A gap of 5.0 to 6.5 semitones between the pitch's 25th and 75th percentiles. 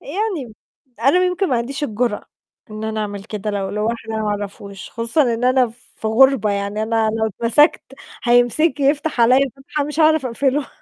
No: average, 4.4 semitones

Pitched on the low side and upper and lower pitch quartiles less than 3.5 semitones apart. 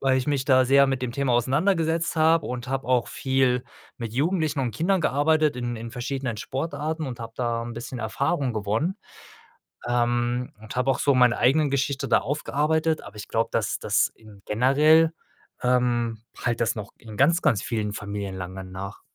No: low, 125 Hz; average, 3.8 semitones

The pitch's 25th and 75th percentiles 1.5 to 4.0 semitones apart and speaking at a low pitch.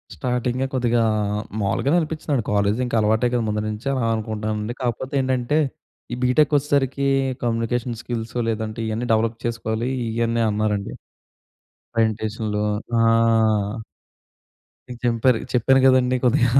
Yes: narrow, 2.5 semitones; low, 115 Hz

